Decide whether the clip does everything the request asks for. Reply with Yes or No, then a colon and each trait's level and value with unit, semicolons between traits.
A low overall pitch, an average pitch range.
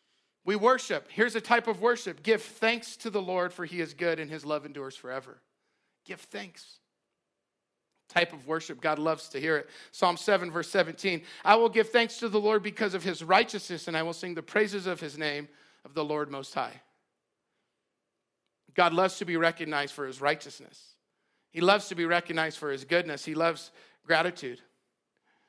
No: medium, 175 Hz; average, 5.0 semitones